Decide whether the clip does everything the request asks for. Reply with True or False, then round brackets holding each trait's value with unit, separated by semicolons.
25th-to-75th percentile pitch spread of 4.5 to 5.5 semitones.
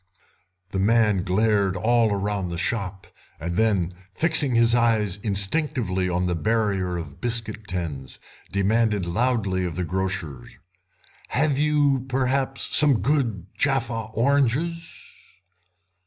True (5.2 semitones)